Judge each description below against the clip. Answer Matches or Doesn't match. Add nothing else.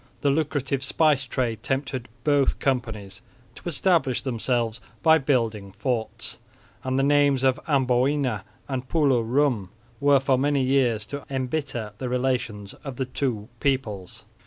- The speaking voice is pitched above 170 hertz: Doesn't match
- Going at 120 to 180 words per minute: Matches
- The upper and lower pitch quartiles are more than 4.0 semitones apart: Doesn't match